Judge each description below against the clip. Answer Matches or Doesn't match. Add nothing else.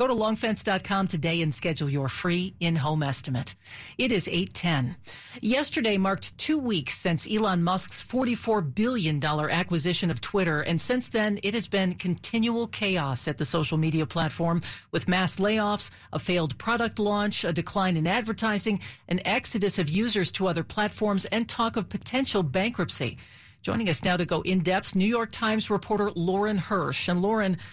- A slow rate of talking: Doesn't match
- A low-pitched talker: Doesn't match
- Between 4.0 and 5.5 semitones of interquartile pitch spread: Matches